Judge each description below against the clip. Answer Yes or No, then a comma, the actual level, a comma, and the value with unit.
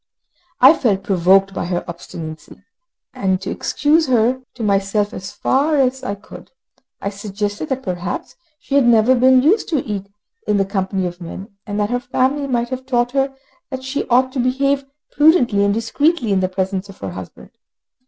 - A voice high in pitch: Yes, high, 225 Hz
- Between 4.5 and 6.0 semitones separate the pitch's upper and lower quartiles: Yes, average, 5.2 semitones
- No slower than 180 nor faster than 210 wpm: Yes, average, 185 wpm